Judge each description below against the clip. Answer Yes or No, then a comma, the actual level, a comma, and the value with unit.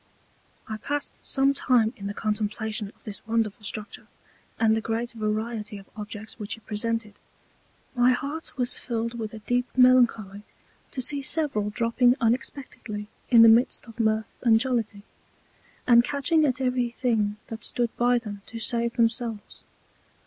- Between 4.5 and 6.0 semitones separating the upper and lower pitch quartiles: No, narrow, 2.4 semitones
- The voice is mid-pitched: No, high, 230 Hz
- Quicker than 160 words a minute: No, average, 155 wpm